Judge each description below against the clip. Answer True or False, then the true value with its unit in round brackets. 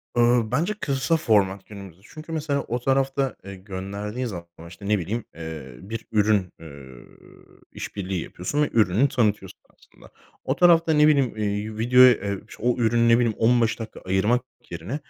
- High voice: False (110 Hz)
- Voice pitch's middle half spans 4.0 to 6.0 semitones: True (4.8 semitones)